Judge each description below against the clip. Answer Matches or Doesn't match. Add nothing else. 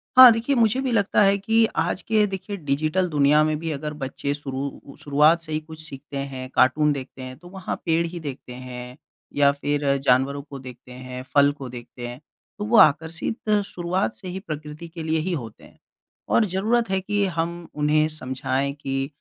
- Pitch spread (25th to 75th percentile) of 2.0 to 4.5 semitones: Doesn't match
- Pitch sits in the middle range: Matches